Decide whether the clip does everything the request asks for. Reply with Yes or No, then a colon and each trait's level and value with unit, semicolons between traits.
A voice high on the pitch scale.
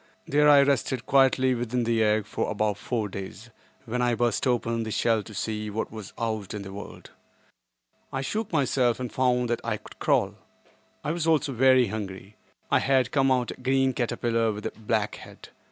No: low, 120 Hz